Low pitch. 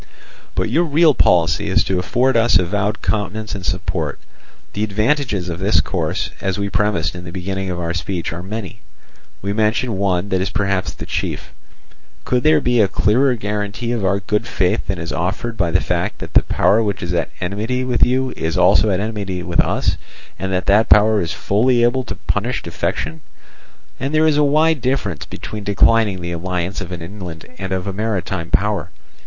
Yes: low, 100 Hz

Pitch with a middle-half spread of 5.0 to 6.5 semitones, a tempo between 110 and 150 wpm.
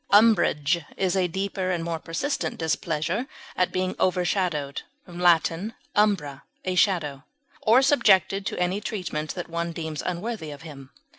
No: average, 3.4 semitones; average, 140 wpm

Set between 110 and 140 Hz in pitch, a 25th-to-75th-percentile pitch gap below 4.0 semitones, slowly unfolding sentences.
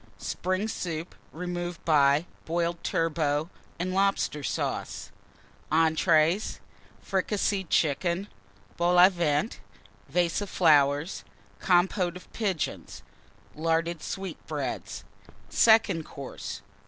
No: medium, 170 Hz; average, 2.8 semitones; slow, 90 wpm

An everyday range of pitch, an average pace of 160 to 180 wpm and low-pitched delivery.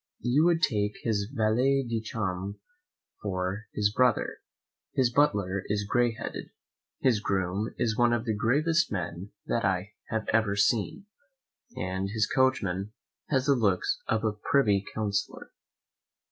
No: average, 3.4 semitones; average, 140 wpm; low, 110 Hz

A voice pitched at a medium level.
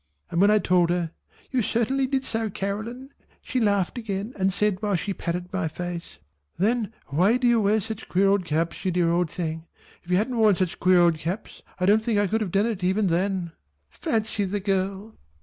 No: high, 195 Hz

